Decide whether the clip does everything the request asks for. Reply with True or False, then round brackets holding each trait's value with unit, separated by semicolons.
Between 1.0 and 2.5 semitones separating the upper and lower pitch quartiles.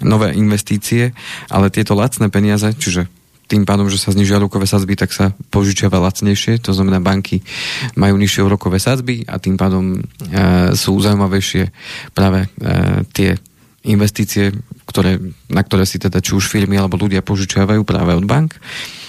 True (1.6 semitones)